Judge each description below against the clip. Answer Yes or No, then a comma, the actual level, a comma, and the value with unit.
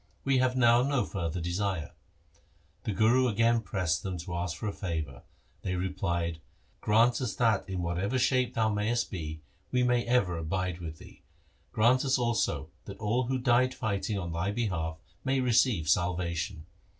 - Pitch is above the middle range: No, low, 100 Hz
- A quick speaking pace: No, average, 170 wpm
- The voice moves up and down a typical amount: No, wide, 5.7 semitones